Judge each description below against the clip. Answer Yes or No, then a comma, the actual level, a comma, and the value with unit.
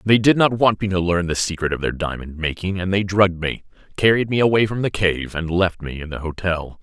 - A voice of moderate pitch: No, very low, 90 Hz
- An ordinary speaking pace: No, fast, 255 wpm